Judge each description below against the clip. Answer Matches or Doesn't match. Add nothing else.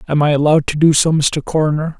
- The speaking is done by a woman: Doesn't match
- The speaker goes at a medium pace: Doesn't match